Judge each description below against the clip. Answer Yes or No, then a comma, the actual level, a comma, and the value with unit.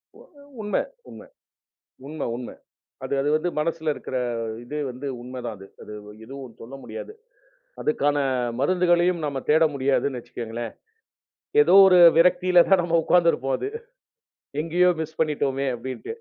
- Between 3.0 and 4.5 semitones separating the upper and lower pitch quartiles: No, average, 5.0 semitones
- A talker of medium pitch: Yes, medium, 150 Hz